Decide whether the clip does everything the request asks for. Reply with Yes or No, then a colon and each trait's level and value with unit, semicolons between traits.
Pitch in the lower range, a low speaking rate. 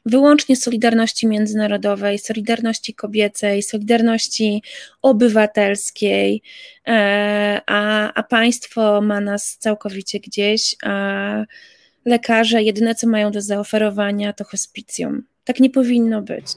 No: high, 215 Hz; slow, 100 wpm